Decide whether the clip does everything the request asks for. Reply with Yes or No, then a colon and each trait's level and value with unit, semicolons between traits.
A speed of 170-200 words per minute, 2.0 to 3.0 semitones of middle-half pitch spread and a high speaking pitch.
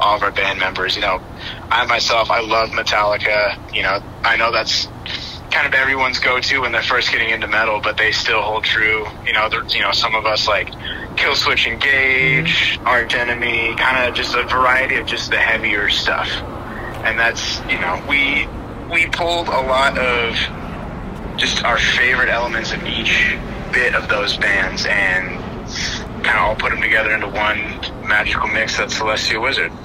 No: average, 180 wpm; narrow, 2.5 semitones; low, 110 Hz